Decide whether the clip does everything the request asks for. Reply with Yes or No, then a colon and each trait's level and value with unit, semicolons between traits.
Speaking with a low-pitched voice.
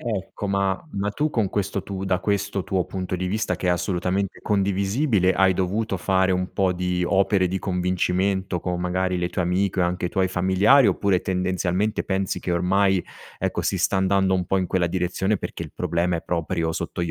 Yes: very low, 95 Hz